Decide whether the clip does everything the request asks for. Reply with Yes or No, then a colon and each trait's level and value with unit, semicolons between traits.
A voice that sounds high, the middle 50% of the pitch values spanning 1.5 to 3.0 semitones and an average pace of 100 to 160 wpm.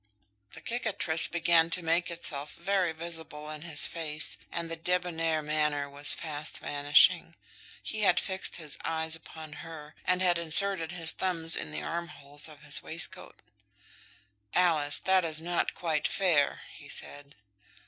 No: medium, 165 Hz; narrow, 2.4 semitones; average, 150 wpm